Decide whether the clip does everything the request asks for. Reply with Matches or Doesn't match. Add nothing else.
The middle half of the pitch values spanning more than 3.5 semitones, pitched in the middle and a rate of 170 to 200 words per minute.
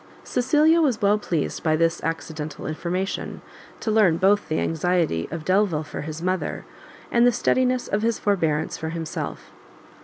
Doesn't match